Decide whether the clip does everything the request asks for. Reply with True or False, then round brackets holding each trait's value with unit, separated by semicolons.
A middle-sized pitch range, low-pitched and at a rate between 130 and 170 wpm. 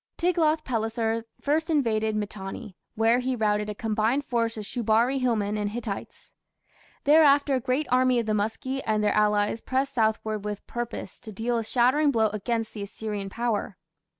False (3.1 semitones; 225 Hz; 165 wpm)